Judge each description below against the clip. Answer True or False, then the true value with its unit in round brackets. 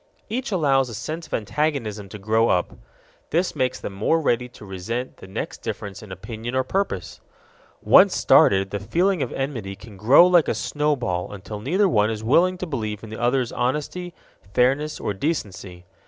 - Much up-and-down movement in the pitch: True (6.6 semitones)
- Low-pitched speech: True (120 Hz)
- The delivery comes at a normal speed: True (180 wpm)